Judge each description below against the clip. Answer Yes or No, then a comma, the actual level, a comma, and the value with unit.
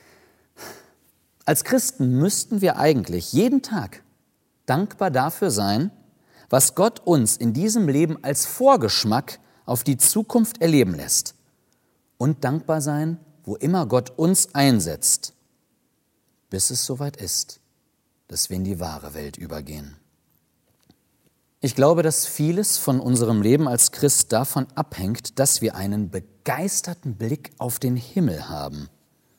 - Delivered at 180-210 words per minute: No, slow, 125 wpm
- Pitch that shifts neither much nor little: No, wide, 8.5 semitones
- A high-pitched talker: No, low, 135 Hz